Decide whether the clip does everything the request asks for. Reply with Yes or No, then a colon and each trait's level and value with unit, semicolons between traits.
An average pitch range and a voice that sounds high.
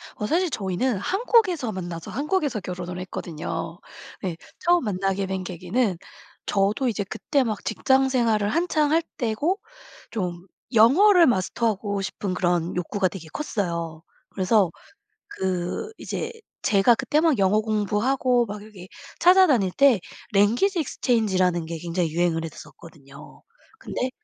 No: wide, 6.5 semitones; high, 205 Hz